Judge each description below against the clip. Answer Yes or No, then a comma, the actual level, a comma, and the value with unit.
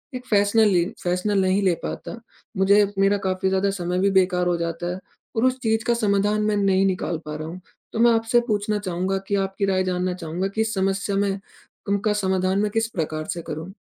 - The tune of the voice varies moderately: No, narrow, 2.3 semitones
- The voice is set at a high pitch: Yes, high, 195 Hz